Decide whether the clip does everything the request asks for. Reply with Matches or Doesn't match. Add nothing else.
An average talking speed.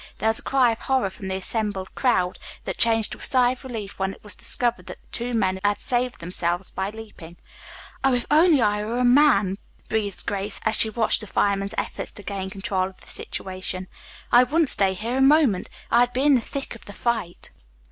Doesn't match